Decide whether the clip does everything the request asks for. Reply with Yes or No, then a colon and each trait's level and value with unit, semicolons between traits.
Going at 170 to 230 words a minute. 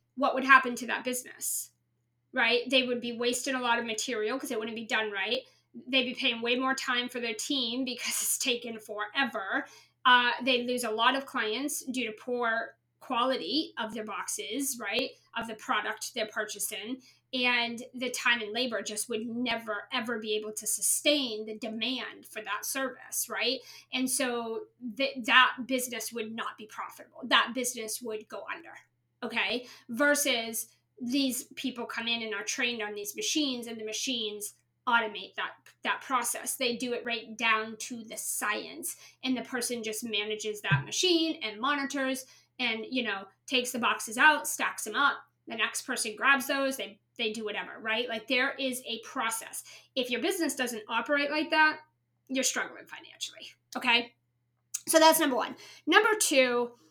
Yes: average, 175 wpm